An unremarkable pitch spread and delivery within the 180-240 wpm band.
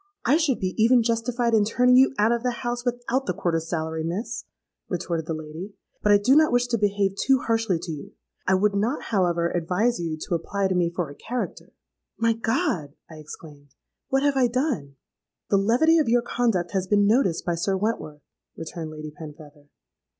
No: wide, 6.3 semitones; average, 190 wpm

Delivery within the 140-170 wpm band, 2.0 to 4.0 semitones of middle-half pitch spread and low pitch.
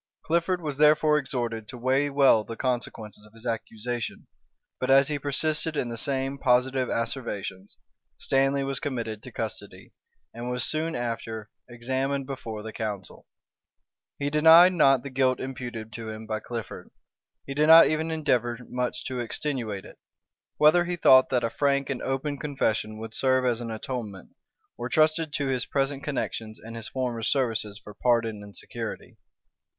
Yes: average, 165 wpm; average, 3.7 semitones; low, 125 Hz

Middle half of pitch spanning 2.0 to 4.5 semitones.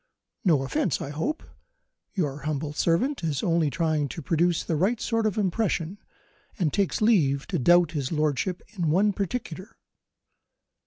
No: average, 4.9 semitones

